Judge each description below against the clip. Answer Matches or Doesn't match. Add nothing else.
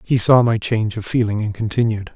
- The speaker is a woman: Doesn't match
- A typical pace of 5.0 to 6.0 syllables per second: Matches